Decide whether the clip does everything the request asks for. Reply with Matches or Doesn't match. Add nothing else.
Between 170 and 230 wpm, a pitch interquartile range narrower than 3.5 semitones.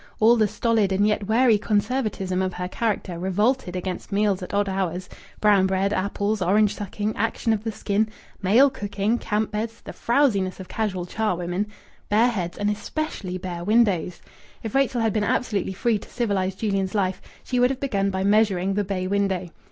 Matches